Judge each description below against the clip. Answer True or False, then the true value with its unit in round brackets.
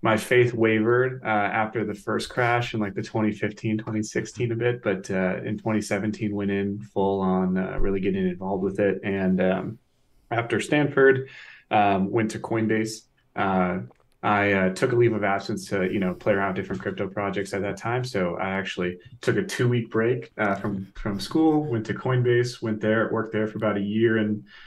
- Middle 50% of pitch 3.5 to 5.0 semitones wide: False (2.9 semitones)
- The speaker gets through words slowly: False (195 wpm)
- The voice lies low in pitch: True (105 Hz)